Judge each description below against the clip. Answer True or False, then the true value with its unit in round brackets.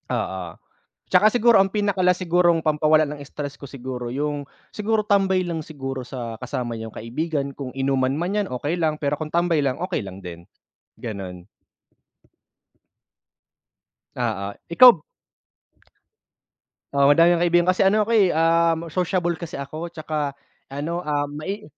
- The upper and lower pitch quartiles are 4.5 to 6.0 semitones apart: True (4.8 semitones)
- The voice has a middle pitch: True (155 Hz)